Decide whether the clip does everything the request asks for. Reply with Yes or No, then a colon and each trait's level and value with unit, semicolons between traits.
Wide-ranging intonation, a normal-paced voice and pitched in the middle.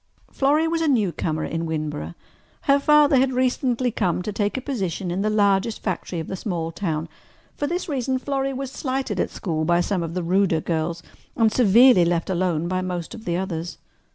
No: wide, 7.1 semitones; average, 195 wpm; high, 195 Hz